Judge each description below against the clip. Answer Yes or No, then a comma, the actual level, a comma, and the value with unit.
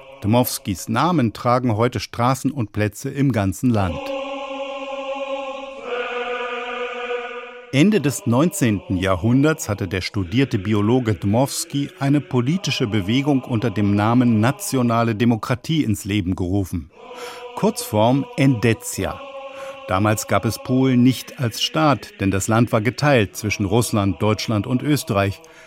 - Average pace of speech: No, slow, 115 wpm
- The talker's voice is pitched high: No, low, 125 Hz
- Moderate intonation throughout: No, wide, 7.7 semitones